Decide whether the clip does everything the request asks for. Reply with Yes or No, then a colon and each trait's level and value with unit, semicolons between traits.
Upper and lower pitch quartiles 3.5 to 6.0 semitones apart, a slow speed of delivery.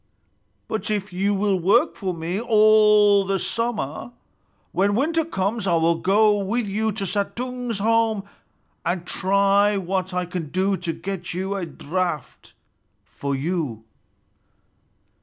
No: average, 2.9 semitones; slow, 130 wpm